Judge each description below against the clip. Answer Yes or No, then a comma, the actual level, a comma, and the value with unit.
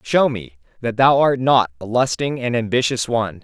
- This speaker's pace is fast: No, average, 190 wpm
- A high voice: No, low, 120 Hz